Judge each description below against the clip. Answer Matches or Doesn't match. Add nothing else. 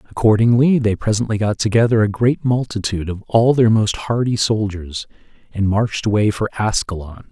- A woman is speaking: Doesn't match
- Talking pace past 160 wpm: Doesn't match